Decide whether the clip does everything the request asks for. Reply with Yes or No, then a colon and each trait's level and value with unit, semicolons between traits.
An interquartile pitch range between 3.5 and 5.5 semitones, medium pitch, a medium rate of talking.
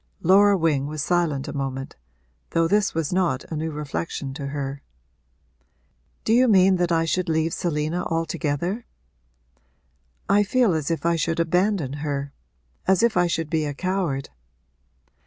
Yes: average, 4.0 semitones; medium, 165 Hz; average, 155 wpm